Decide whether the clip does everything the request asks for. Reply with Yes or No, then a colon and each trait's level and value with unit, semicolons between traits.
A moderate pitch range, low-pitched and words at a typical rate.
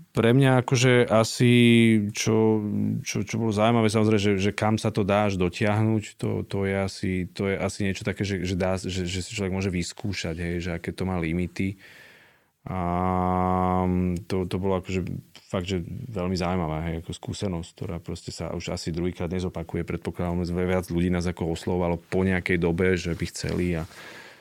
No: average, 3.1 semitones; very low, 95 Hz; fast, 180 wpm